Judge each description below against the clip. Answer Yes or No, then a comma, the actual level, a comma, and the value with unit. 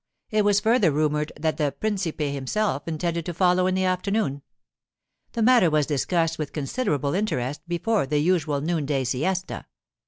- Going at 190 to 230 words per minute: No, average, 155 wpm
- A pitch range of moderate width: Yes, average, 4.5 semitones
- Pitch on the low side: No, medium, 165 Hz